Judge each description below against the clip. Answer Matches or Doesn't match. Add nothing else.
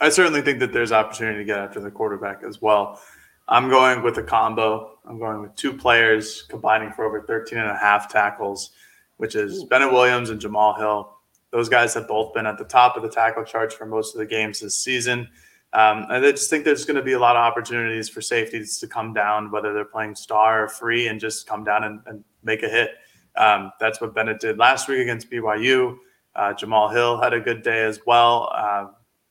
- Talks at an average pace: Doesn't match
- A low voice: Matches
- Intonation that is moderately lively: Doesn't match